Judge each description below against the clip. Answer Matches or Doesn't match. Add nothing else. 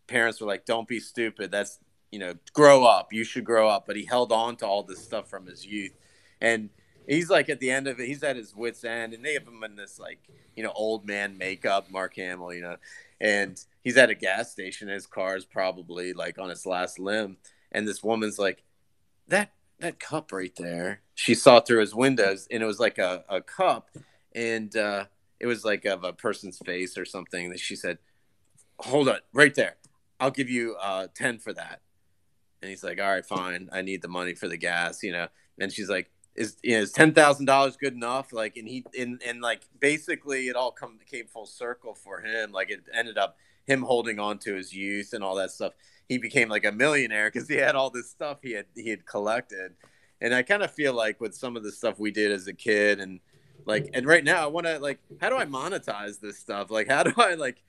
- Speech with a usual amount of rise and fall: Matches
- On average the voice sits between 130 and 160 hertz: Doesn't match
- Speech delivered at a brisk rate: Matches